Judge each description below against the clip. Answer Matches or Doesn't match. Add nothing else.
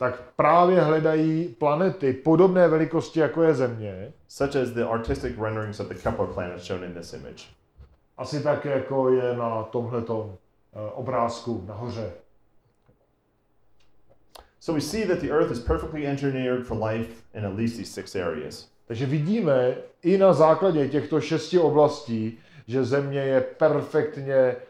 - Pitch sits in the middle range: Doesn't match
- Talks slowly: Matches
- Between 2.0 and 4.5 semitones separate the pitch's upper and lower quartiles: Doesn't match